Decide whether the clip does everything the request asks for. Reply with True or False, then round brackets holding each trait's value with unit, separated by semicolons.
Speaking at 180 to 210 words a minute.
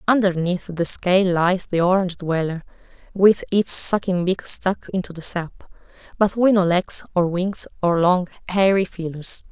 False (160 wpm)